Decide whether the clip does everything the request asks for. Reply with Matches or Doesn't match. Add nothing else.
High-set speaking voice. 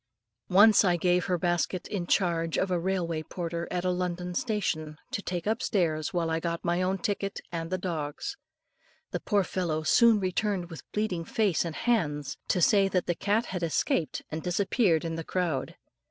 Doesn't match